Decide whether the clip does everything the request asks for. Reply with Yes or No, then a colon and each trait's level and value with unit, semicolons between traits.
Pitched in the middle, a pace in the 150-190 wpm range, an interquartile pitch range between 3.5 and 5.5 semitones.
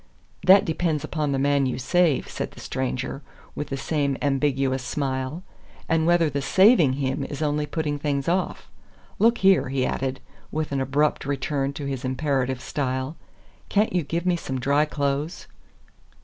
No: medium, 145 Hz; average, 165 wpm; average, 2.9 semitones